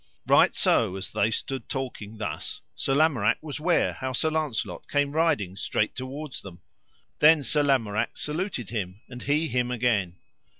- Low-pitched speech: Yes, low, 130 Hz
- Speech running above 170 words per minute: No, average, 160 wpm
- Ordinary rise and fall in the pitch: No, wide, 5.7 semitones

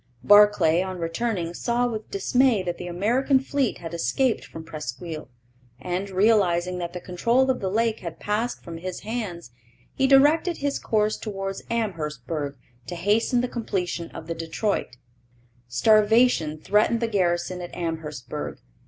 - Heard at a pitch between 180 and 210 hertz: Yes, high, 190 Hz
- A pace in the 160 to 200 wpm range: No, average, 145 wpm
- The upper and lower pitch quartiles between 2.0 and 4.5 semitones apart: No, average, 5.3 semitones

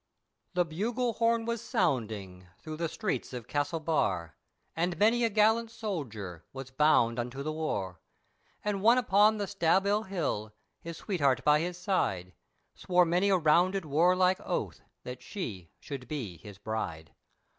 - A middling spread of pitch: No, wide, 8.4 semitones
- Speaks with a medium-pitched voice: Yes, medium, 165 Hz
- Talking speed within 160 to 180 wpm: No, average, 145 wpm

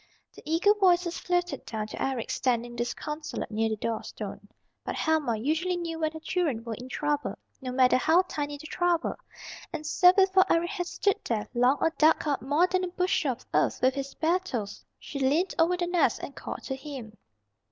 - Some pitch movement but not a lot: No, wide, 5.7 semitones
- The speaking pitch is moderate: No, very high, 305 Hz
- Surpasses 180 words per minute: Yes, average, 200 wpm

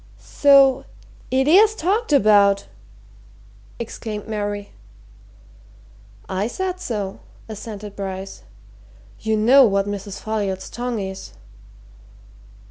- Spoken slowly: Yes, slow, 90 wpm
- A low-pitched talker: No, high, 215 Hz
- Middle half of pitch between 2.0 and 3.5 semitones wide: No, average, 5.0 semitones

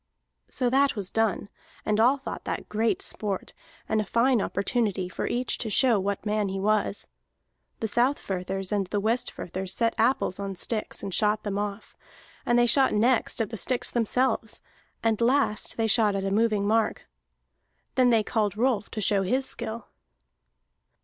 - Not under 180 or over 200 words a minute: No, average, 170 wpm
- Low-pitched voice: No, high, 215 Hz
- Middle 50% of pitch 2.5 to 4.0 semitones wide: Yes, average, 3.0 semitones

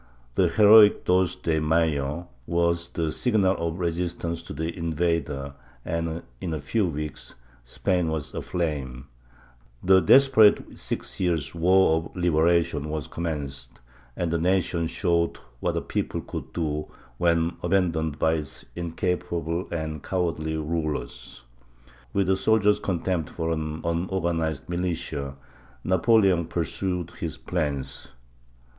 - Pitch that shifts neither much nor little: No, narrow, 2.3 semitones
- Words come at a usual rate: No, slow, 125 wpm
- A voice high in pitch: No, very low, 85 Hz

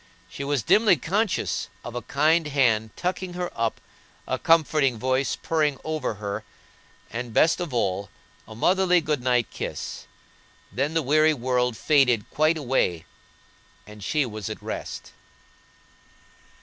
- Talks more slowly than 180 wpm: Yes, slow, 135 wpm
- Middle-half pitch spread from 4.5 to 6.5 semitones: Yes, average, 5.2 semitones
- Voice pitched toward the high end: No, medium, 140 Hz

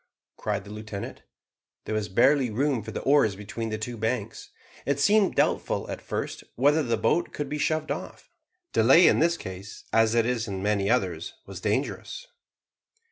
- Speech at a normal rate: Yes, average, 175 wpm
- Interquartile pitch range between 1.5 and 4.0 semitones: No, average, 5.2 semitones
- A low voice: Yes, low, 115 Hz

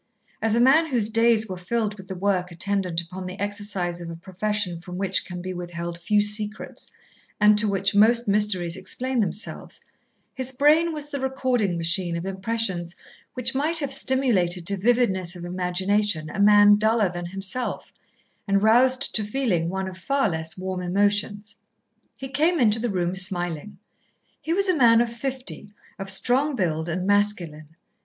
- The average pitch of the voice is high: Yes, high, 205 Hz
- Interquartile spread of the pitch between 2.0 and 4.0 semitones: No, average, 4.6 semitones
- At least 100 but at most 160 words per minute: No, average, 170 wpm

